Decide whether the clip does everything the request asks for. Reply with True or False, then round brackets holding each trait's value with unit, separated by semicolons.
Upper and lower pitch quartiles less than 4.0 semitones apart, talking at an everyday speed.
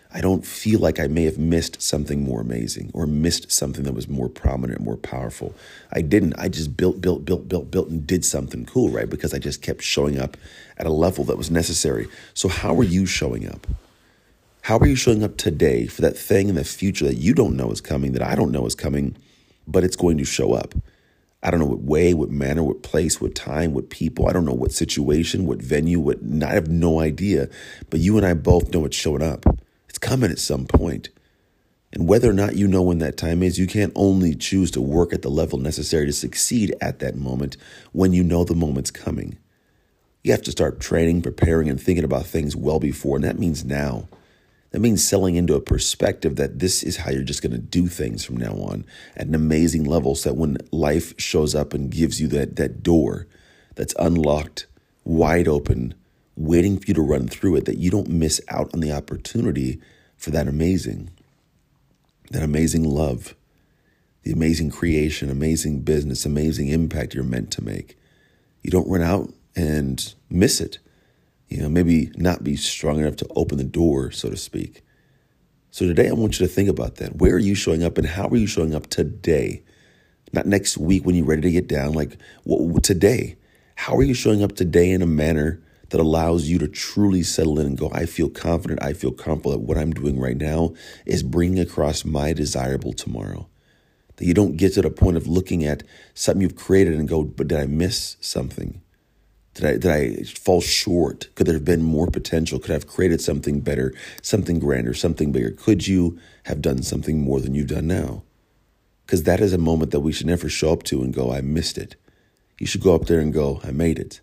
False (3.4 semitones; 215 wpm)